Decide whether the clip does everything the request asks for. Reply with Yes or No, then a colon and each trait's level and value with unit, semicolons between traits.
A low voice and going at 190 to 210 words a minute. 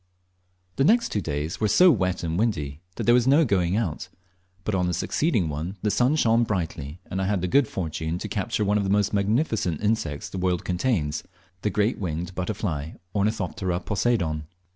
Yes: very low, 95 Hz; average, 195 wpm